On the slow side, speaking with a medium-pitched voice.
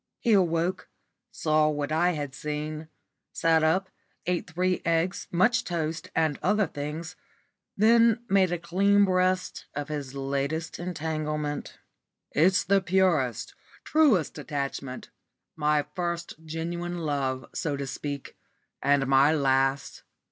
Yes: slow, 120 wpm; medium, 160 Hz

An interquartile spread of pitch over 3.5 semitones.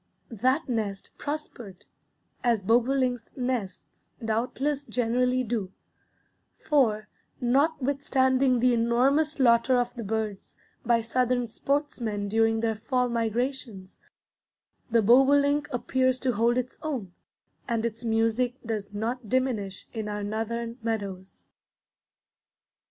No: average, 2.7 semitones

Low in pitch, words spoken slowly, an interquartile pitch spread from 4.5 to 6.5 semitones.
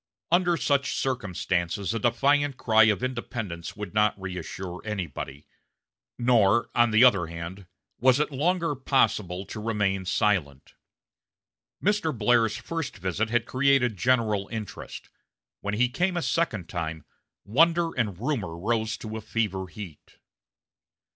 Yes: low, 110 Hz; slow, 130 wpm; average, 5.2 semitones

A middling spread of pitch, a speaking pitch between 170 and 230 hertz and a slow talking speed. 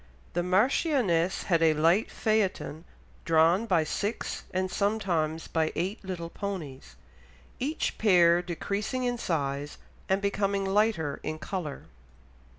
Yes: average, 3.9 semitones; medium, 185 Hz; slow, 120 wpm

